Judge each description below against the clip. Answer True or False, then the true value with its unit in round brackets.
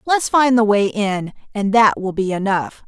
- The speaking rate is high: True (210 wpm)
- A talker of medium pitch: False (215 Hz)